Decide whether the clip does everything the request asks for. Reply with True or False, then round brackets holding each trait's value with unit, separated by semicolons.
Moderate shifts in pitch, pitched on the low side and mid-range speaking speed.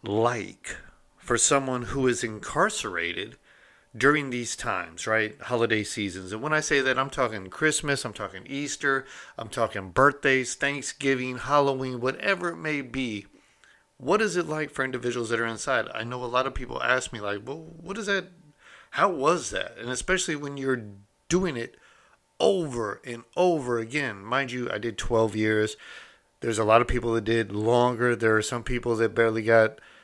True (3.7 semitones; 125 Hz; 175 wpm)